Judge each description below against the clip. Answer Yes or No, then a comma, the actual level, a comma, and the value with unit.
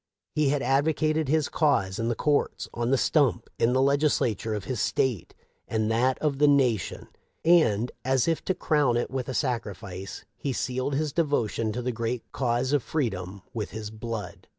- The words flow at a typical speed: Yes, average, 180 wpm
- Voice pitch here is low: Yes, low, 125 Hz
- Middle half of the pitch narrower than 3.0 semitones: No, average, 4.2 semitones